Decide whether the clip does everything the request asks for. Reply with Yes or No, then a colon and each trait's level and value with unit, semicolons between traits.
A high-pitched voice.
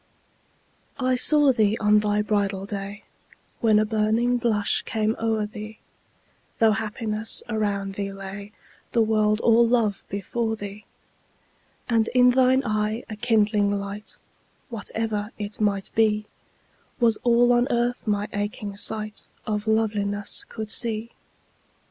Yes: high, 215 Hz